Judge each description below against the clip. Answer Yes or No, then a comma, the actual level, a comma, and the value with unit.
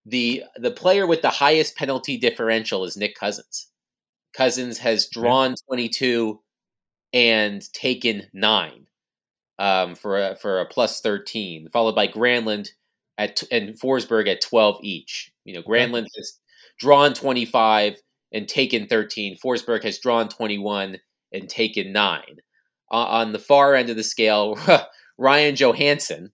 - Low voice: Yes, low, 115 Hz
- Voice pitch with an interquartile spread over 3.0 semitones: Yes, average, 3.5 semitones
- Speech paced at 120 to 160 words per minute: Yes, average, 145 wpm